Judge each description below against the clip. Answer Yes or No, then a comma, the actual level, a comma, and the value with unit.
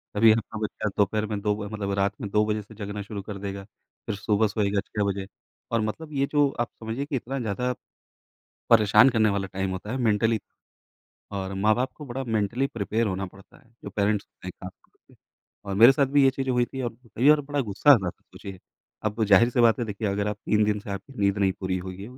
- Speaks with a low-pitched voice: Yes, low, 105 Hz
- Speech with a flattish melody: No, average, 3.2 semitones